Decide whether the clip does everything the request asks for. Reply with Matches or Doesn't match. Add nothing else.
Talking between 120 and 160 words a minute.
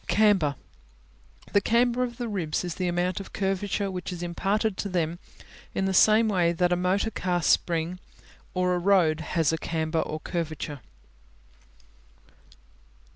Matches